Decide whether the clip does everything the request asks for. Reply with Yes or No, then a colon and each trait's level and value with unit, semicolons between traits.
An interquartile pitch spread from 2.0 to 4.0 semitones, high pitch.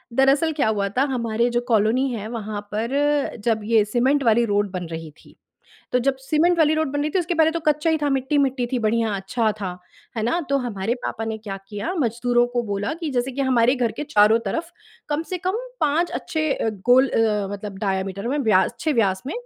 No: average, 5.1 semitones; high, 240 Hz